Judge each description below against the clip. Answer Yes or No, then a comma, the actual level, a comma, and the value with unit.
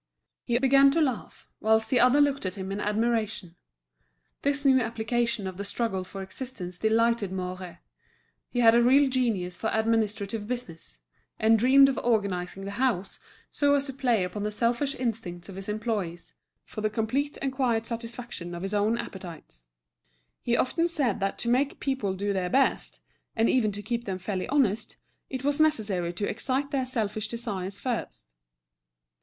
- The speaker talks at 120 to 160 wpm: No, average, 170 wpm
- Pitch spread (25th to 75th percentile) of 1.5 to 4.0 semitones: No, average, 4.6 semitones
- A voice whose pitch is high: Yes, high, 225 Hz